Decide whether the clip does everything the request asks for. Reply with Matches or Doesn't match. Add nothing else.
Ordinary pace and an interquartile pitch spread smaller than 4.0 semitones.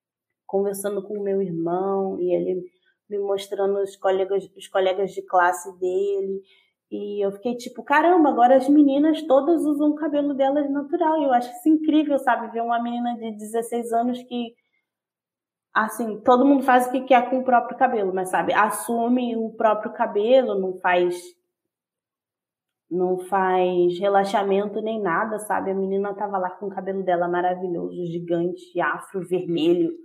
Doesn't match